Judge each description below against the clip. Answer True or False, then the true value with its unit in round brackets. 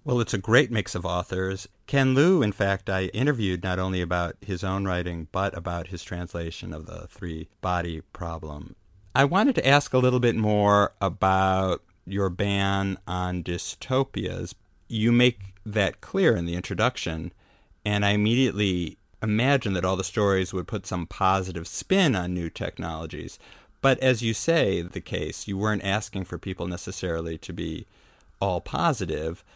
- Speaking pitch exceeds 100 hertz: False (95 Hz)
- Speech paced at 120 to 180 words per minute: True (160 wpm)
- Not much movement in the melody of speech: False (3.3 semitones)